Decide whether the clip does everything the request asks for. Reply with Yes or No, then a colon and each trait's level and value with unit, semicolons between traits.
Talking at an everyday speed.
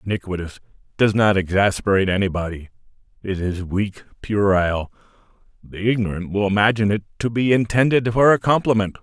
No: slow, 125 wpm